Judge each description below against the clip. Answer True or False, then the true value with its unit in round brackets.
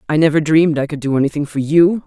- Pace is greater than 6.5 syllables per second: True (6.9 syllables/s)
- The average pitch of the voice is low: False (150 Hz)